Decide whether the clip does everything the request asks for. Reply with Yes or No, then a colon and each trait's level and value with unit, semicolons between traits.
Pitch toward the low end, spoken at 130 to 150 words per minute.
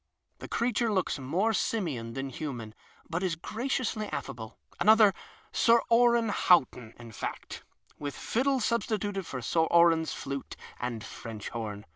No: medium, 170 Hz; average, 145 wpm